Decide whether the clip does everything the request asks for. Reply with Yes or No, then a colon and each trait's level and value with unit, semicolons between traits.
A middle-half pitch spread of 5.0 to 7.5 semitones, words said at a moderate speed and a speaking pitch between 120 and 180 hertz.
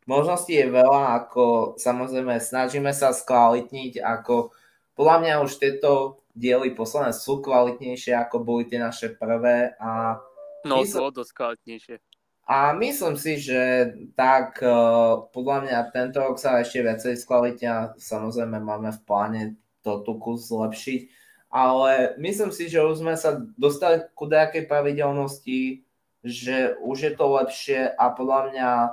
No: average, 2.8 semitones; average, 140 wpm; low, 125 Hz